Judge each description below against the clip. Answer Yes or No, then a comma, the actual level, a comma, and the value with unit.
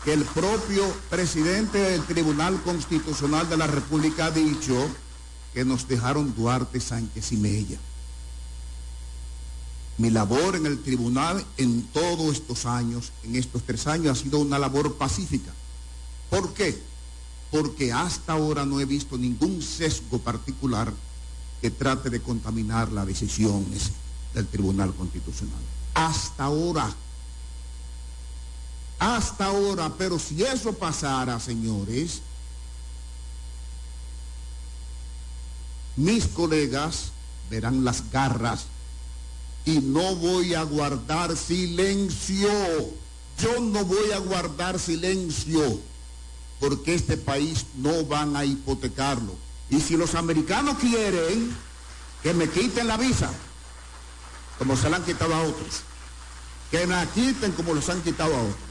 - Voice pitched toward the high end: No, low, 125 Hz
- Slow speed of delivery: Yes, slow, 120 wpm